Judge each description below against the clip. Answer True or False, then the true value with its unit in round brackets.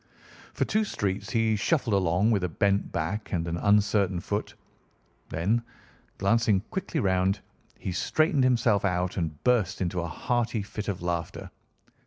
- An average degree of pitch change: True (4.0 semitones)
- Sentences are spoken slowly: False (150 wpm)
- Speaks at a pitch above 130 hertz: False (100 Hz)